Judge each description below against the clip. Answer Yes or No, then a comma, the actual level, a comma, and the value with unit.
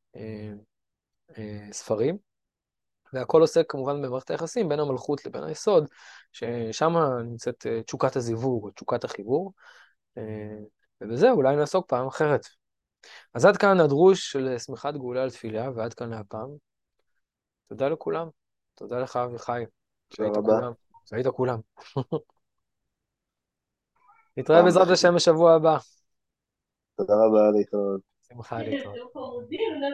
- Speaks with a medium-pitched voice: No, low, 130 Hz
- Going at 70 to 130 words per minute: Yes, slow, 100 wpm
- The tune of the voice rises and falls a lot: Yes, wide, 6.0 semitones